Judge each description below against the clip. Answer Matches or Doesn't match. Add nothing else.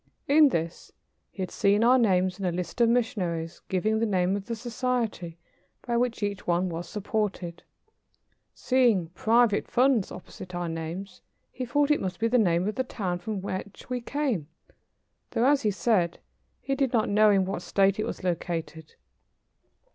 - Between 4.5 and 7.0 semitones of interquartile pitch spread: Matches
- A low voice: Doesn't match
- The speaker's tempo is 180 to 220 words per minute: Doesn't match